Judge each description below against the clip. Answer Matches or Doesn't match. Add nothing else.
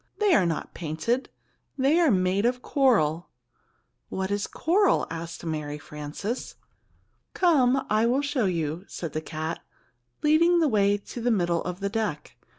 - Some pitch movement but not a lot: Doesn't match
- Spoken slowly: Doesn't match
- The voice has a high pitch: Matches